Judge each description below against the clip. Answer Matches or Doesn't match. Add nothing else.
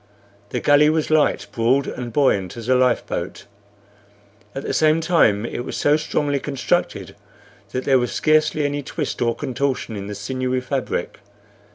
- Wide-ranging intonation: Doesn't match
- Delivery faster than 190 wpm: Doesn't match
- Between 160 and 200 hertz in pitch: Doesn't match